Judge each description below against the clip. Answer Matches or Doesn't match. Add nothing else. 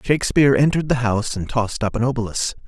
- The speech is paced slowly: Doesn't match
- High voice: Doesn't match